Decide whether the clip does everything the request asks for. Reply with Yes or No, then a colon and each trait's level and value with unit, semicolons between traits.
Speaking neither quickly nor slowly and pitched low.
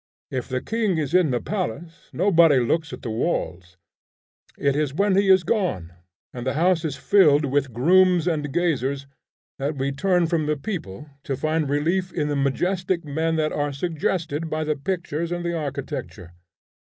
No: average, 175 wpm; medium, 155 Hz